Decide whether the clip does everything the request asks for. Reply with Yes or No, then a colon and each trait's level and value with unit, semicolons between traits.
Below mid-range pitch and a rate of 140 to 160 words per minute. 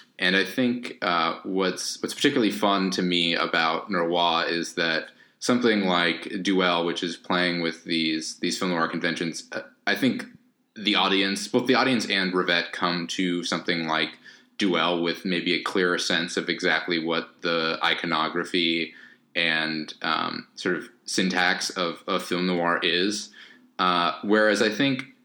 Yes: very low, 90 Hz; average, 150 wpm